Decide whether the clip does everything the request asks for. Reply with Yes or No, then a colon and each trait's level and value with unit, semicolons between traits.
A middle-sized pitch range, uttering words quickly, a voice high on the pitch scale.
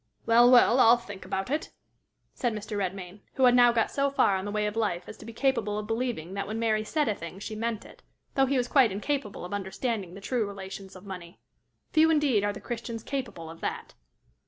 Yes: average, 3.8 semitones; fast, 230 wpm; high, 215 Hz